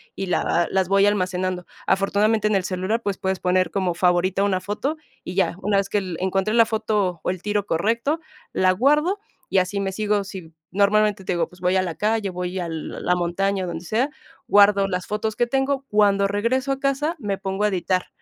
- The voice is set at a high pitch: Yes, high, 195 Hz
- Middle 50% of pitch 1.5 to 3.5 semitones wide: Yes, narrow, 2.5 semitones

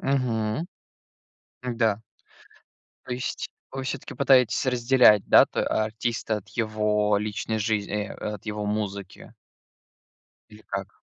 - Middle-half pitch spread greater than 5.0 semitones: No, narrow, 2.6 semitones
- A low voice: Yes, low, 110 Hz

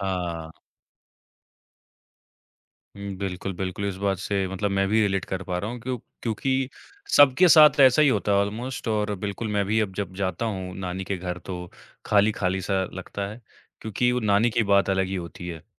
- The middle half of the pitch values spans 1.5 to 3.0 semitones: Yes, average, 2.7 semitones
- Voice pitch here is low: Yes, low, 100 Hz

